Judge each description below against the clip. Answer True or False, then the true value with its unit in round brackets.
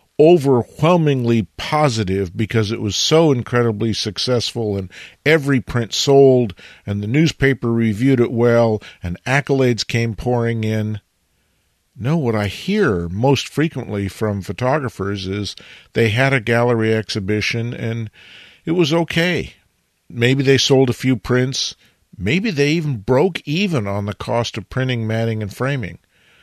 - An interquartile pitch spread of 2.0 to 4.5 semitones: True (4.1 semitones)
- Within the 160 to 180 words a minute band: False (135 wpm)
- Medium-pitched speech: False (120 Hz)